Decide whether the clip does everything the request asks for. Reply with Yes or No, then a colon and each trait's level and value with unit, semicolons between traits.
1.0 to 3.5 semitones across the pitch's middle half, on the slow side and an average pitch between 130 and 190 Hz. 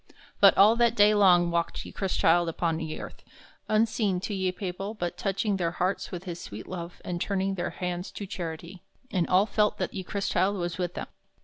No: narrow, 2.5 semitones; average, 200 wpm; medium, 185 Hz